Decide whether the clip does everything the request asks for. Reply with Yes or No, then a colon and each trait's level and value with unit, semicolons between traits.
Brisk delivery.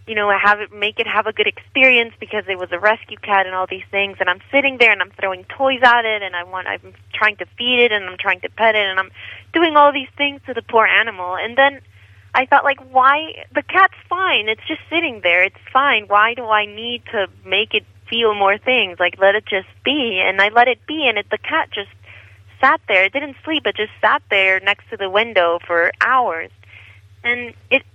Yes: fast, 240 wpm